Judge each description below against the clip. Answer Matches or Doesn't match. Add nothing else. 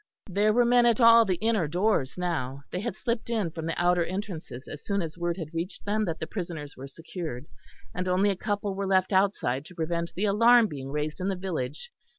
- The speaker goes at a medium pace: Doesn't match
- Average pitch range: Matches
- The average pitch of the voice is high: Doesn't match